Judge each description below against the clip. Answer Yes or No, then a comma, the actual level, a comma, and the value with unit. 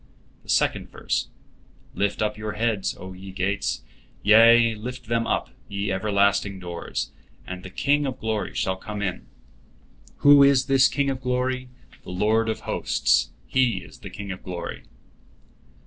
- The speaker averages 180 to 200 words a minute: No, average, 155 wpm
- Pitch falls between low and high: No, low, 105 Hz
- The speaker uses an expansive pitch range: No, average, 4.4 semitones